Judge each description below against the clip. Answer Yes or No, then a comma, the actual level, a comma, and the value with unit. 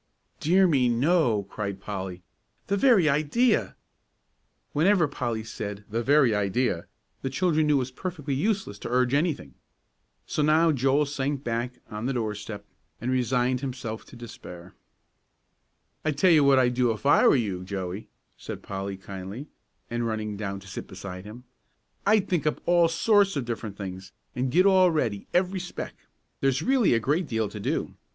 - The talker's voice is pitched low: Yes, low, 125 Hz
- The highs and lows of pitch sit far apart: Yes, wide, 6.5 semitones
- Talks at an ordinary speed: Yes, average, 170 wpm